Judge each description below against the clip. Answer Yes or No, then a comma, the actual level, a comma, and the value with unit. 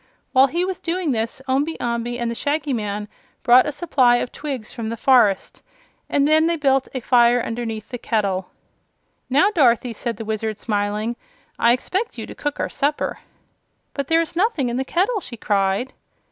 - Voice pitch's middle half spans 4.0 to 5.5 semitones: Yes, average, 4.6 semitones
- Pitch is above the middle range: Yes, very high, 250 Hz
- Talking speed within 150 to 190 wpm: Yes, average, 185 wpm